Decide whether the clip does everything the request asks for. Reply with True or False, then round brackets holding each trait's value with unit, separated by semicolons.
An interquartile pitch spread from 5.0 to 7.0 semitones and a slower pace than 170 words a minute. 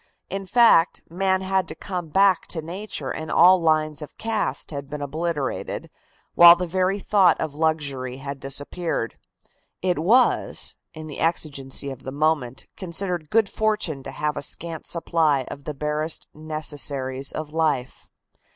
False (4.2 semitones; 150 wpm)